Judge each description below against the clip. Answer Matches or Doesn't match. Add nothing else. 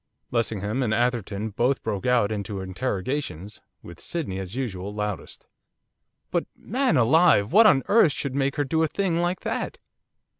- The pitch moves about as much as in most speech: Doesn't match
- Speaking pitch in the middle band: Doesn't match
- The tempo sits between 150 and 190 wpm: Matches